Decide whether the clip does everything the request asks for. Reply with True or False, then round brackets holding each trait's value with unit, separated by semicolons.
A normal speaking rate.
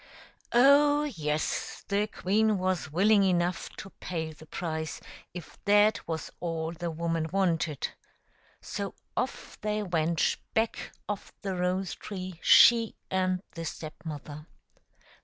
False (125 wpm)